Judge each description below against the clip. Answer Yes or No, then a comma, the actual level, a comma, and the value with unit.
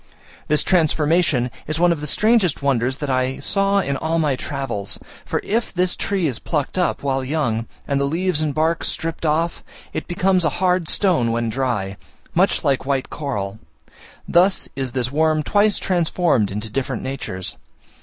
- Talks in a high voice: No, medium, 150 Hz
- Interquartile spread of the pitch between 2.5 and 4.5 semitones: No, average, 5.1 semitones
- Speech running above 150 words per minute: Yes, average, 170 wpm